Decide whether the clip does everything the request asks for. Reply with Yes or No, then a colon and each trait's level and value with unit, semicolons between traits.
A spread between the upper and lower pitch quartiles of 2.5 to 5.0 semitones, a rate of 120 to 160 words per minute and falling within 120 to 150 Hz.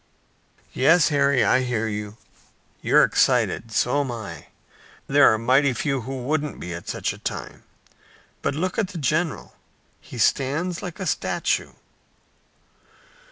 Yes: average, 4.4 semitones; average, 140 wpm; low, 135 Hz